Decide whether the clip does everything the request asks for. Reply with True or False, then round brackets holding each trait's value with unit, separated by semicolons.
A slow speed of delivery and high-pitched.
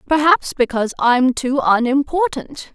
True (110 wpm; 275 Hz)